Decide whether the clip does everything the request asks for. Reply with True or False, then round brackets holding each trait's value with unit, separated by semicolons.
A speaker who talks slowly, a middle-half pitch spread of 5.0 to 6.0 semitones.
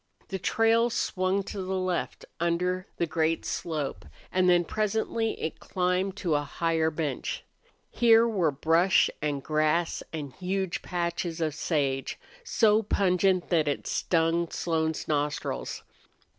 False (130 wpm; 3.2 semitones)